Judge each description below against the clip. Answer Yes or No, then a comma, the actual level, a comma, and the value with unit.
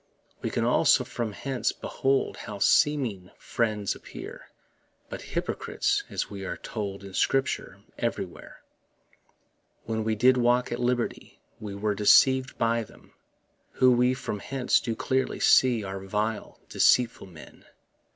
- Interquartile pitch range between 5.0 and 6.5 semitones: No, average, 3.6 semitones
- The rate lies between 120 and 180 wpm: Yes, slow, 135 wpm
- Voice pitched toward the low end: Yes, low, 115 Hz